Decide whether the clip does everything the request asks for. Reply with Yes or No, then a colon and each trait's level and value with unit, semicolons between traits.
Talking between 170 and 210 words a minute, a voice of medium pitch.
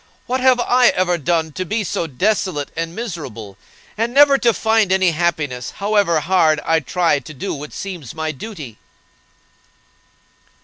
No: average, 150 wpm; medium, 175 Hz